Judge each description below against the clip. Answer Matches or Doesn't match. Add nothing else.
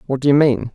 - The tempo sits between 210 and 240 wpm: Doesn't match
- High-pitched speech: Doesn't match